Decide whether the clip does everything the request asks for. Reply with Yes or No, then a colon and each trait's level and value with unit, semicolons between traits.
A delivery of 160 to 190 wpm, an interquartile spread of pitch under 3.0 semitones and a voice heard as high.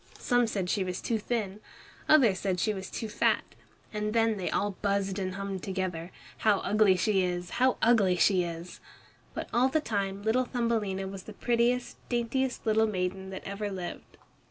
No: average, 180 wpm; average, 3.3 semitones; high, 200 Hz